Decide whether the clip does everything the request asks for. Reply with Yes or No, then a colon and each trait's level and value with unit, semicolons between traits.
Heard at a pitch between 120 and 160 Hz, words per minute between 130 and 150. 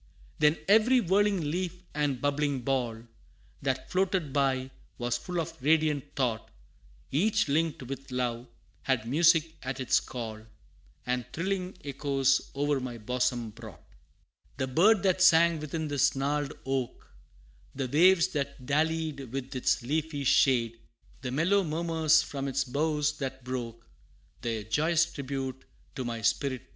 Yes: medium, 140 Hz; average, 140 wpm